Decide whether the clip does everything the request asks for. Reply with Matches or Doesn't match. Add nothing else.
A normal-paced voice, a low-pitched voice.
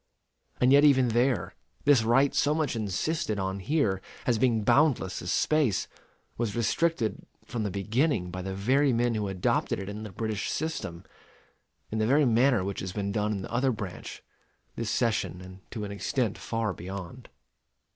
Matches